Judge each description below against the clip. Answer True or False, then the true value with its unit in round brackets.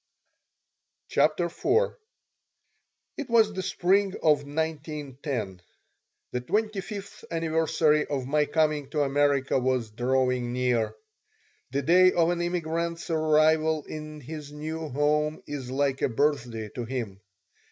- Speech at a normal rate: False (120 wpm)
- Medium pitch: True (150 Hz)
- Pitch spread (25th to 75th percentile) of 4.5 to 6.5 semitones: False (3.7 semitones)